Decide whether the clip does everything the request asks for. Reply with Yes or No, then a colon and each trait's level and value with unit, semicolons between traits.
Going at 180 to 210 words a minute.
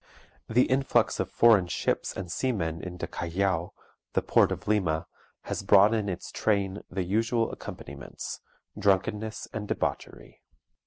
No: slow, 135 wpm